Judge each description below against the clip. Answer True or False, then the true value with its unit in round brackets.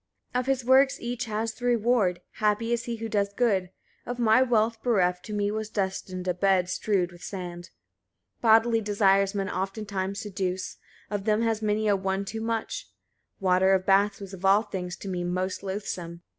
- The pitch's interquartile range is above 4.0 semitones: False (3.0 semitones)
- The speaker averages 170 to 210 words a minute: True (190 wpm)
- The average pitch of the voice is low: False (205 Hz)